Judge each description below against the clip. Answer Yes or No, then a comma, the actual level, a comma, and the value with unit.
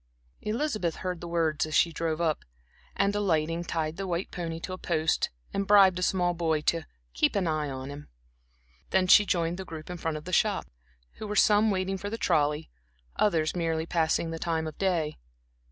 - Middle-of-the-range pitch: Yes, medium, 170 Hz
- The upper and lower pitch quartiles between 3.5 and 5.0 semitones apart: No, average, 3.0 semitones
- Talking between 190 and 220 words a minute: Yes, average, 200 wpm